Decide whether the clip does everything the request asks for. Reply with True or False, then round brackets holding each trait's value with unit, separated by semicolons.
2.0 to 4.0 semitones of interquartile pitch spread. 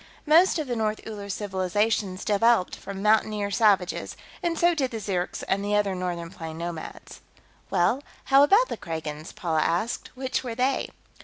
False (5.0 semitones)